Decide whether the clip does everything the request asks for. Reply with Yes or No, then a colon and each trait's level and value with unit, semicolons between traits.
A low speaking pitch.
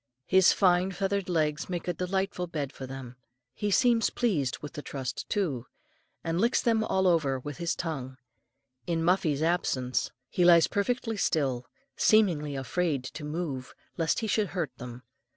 No: medium, 170 Hz